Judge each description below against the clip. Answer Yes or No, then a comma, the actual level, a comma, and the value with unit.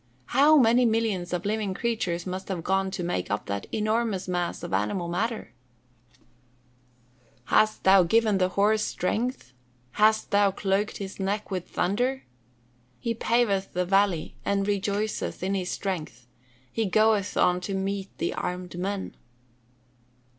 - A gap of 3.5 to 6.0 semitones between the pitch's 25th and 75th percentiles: No, average, 3.1 semitones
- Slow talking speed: No, average, 145 wpm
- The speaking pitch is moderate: No, high, 195 Hz